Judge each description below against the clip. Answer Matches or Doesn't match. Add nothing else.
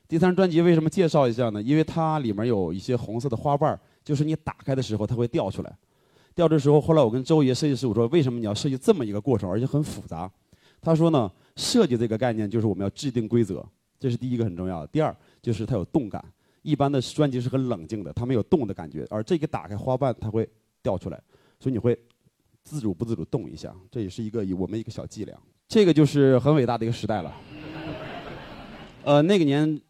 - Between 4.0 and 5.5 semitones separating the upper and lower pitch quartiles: Matches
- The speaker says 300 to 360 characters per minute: Matches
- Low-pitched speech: Matches